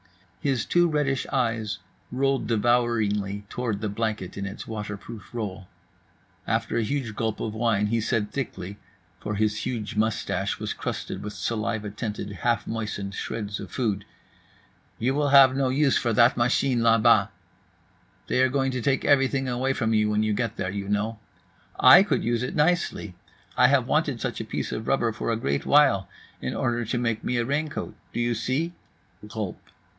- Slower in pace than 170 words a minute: No, average, 180 wpm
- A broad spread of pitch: No, average, 3.6 semitones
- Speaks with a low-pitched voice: Yes, low, 115 Hz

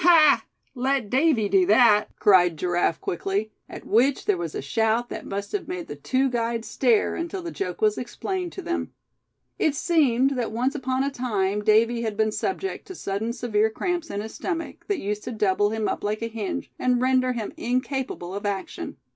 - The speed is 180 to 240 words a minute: Yes, average, 195 wpm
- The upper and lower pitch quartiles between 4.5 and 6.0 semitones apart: Yes, average, 4.9 semitones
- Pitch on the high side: Yes, high, 235 Hz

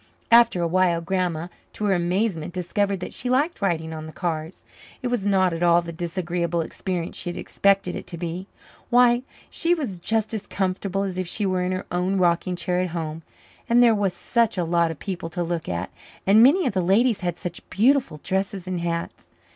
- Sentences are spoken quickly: Yes, fast, 210 wpm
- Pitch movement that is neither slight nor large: Yes, average, 3.0 semitones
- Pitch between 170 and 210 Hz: Yes, medium, 185 Hz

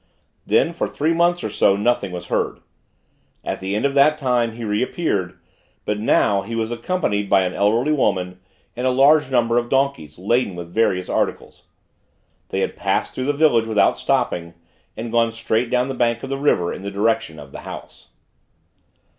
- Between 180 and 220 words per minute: Yes, average, 185 wpm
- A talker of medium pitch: No, low, 115 Hz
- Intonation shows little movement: No, average, 4.7 semitones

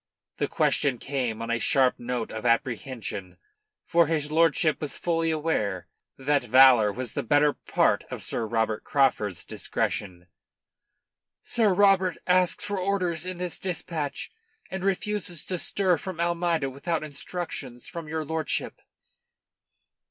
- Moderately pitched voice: Yes, medium, 150 Hz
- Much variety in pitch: Yes, wide, 6.1 semitones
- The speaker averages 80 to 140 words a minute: Yes, slow, 135 wpm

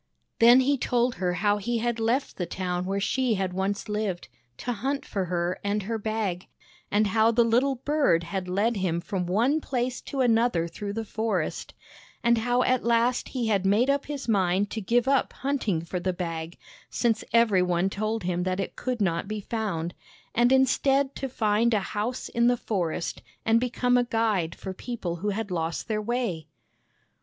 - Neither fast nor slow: Yes, average, 190 wpm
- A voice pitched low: No, high, 215 Hz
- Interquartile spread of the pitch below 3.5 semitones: No, average, 4.5 semitones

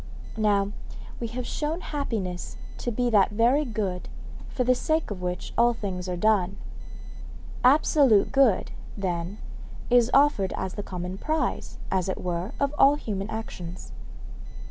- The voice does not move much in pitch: No, average, 5.3 semitones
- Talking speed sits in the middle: Yes, average, 145 wpm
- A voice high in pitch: Yes, high, 215 Hz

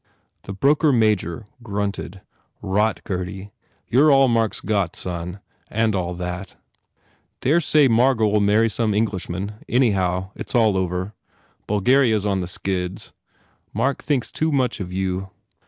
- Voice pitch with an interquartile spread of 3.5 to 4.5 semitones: Yes, average, 3.8 semitones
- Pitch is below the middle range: Yes, low, 105 Hz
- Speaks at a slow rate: No, average, 155 wpm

